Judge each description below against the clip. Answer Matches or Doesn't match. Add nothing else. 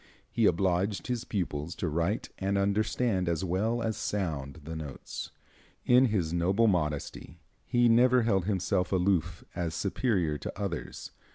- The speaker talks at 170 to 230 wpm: Doesn't match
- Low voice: Matches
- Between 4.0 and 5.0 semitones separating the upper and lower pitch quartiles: Matches